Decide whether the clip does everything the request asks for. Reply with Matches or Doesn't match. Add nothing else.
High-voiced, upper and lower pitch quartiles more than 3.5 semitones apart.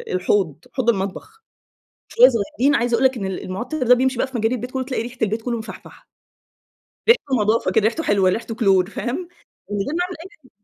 Matches